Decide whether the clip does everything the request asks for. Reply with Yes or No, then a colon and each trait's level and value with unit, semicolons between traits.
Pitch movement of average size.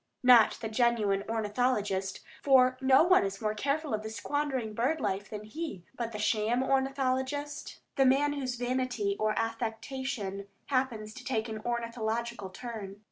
Yes: average, 3.5 semitones